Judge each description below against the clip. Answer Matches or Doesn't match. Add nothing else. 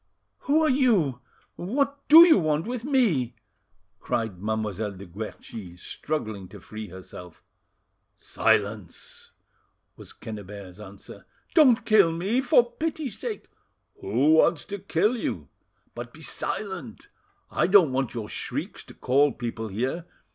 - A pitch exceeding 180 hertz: Doesn't match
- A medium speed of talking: Doesn't match